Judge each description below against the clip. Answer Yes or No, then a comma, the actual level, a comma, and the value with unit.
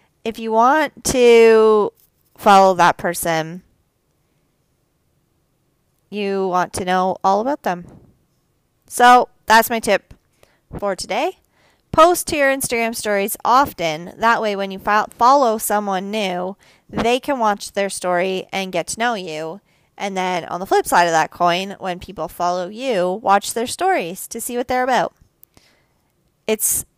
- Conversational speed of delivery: Yes, average, 145 wpm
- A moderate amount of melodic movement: Yes, average, 4.6 semitones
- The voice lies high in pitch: Yes, high, 200 Hz